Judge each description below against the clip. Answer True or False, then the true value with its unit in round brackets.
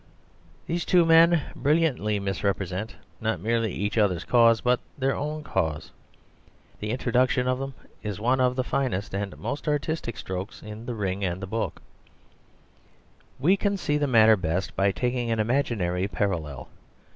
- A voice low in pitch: True (115 Hz)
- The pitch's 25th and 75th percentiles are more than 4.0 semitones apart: True (5.4 semitones)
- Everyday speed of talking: True (155 wpm)